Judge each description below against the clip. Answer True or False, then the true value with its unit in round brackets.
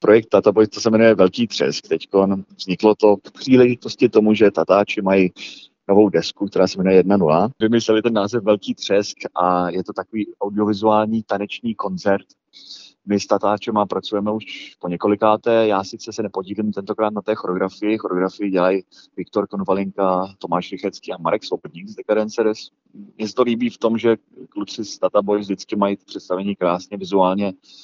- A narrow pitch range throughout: True (2.1 semitones)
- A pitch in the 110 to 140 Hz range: False (100 Hz)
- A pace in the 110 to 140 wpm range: False (165 wpm)